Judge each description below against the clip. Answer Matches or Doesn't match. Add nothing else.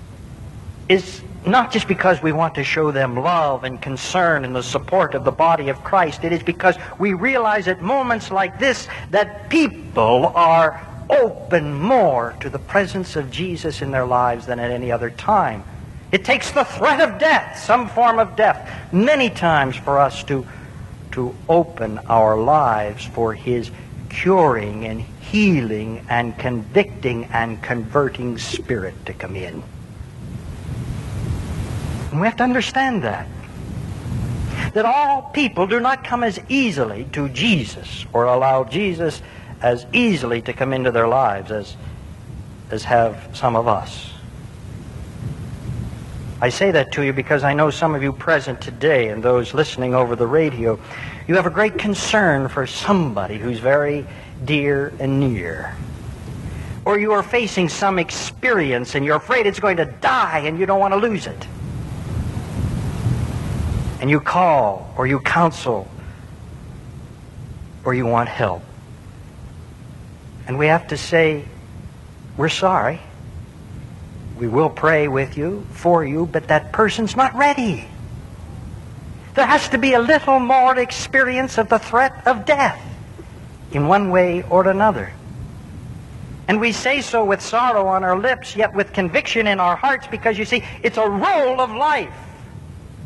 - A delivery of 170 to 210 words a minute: Doesn't match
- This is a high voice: Doesn't match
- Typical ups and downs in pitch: Doesn't match